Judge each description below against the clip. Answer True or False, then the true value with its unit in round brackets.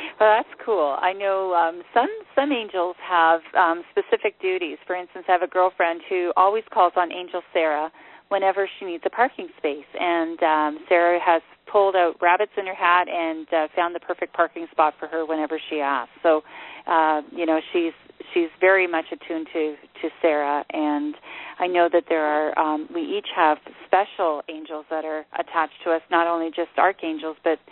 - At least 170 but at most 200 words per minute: True (190 wpm)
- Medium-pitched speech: True (175 Hz)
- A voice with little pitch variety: False (3.1 semitones)